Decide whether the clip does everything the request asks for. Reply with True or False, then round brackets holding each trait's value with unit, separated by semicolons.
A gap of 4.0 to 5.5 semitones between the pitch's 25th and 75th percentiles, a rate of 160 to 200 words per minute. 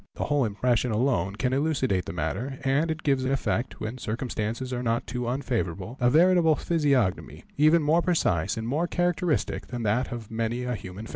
True (4.7 semitones; 190 wpm)